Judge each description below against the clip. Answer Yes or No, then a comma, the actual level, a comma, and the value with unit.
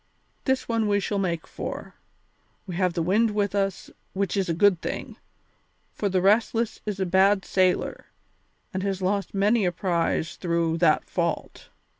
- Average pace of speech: Yes, average, 165 wpm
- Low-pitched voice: No, high, 195 Hz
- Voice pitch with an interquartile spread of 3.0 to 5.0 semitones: No, narrow, 2.4 semitones